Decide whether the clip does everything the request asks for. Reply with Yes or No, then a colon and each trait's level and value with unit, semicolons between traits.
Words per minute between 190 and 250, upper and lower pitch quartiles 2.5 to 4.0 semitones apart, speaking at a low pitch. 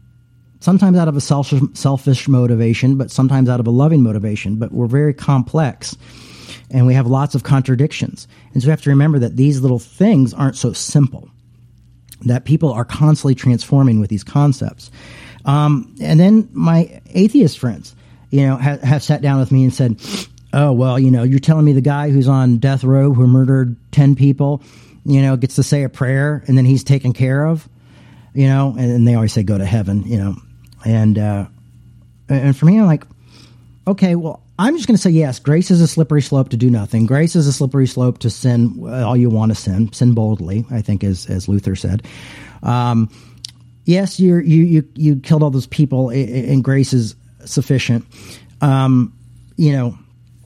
Yes: average, 195 wpm; average, 3.0 semitones; low, 130 Hz